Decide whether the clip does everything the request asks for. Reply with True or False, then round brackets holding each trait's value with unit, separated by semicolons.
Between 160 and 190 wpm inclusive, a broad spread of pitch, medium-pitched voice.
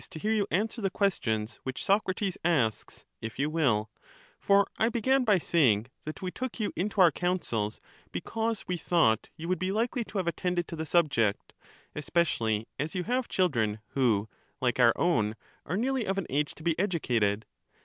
True (185 wpm; 8.9 semitones; 170 Hz)